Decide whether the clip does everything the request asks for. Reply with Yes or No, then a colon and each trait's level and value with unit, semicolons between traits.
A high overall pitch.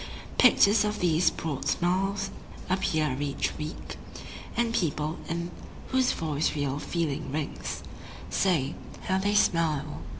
No: medium, 165 Hz